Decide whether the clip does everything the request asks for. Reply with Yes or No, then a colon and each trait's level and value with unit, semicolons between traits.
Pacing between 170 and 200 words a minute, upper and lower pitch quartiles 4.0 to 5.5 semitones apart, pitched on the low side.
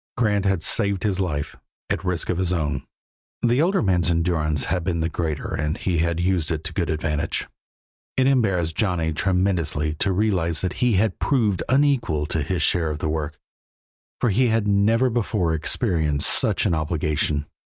Yes: average, 175 wpm; average, 4.5 semitones; very low, 90 Hz